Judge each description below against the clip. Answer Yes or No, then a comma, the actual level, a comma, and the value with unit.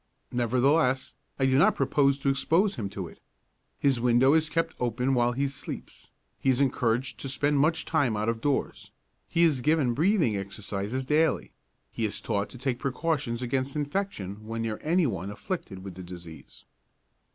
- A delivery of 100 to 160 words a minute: No, average, 175 wpm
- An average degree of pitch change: Yes, average, 4.5 semitones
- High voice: No, low, 130 Hz